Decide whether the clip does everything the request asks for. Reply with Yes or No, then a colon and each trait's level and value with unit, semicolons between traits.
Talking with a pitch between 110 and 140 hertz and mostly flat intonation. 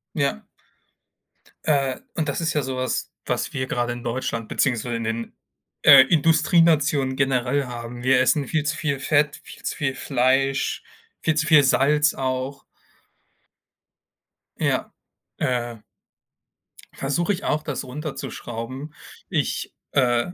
No: low, 135 Hz; average, 3.0 semitones